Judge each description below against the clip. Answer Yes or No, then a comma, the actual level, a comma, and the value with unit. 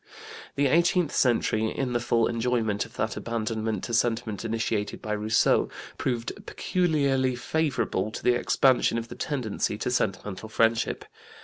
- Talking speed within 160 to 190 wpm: No, average, 140 wpm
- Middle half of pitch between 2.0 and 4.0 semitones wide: Yes, average, 3.0 semitones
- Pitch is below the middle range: Yes, low, 115 Hz